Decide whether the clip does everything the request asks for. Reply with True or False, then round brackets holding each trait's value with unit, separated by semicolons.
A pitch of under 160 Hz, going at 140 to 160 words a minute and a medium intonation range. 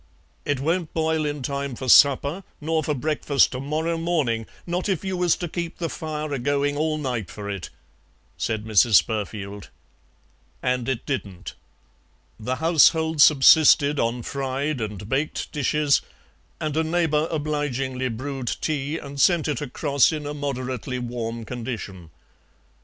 True (140 Hz; 145 wpm; 4.0 semitones)